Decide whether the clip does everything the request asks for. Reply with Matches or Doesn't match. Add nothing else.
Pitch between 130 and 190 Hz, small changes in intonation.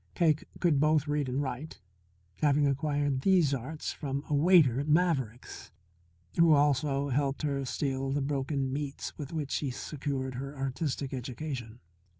Matches